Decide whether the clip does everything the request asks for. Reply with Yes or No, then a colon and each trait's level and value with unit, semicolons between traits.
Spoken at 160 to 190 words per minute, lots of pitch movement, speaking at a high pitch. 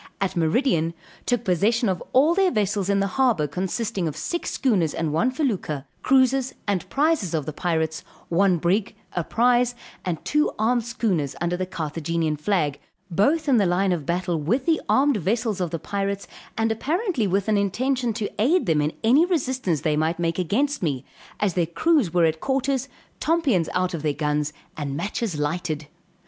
Yes: average, 180 wpm; wide, 7.1 semitones; high, 195 Hz